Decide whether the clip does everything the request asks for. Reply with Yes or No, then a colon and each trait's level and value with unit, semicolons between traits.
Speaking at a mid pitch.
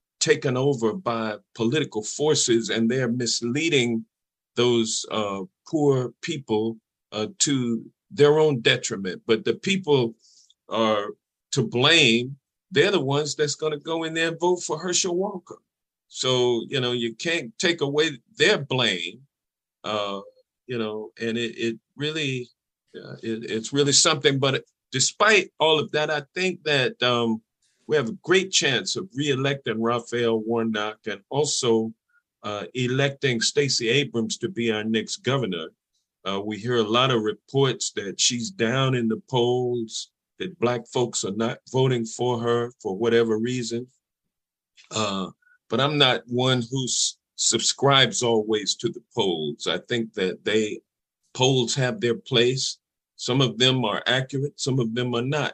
No: low, 125 Hz